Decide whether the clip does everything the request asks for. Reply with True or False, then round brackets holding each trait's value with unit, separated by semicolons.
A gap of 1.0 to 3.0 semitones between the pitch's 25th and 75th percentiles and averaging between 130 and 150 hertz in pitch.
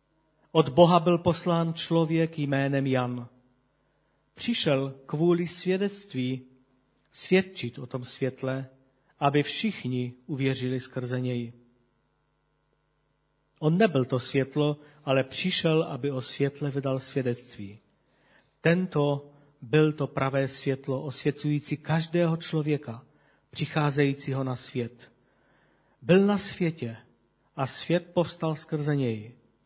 False (3.5 semitones; 140 Hz)